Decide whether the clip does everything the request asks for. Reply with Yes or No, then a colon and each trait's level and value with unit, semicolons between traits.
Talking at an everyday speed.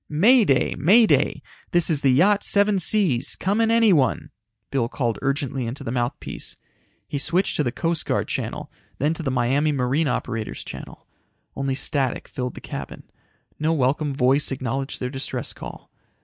Yes: average, 165 wpm